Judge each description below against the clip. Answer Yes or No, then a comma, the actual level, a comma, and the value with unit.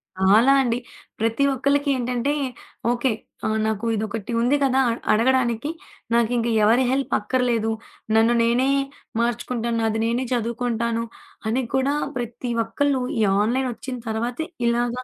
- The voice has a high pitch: Yes, high, 240 Hz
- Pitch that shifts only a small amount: Yes, narrow, 2.3 semitones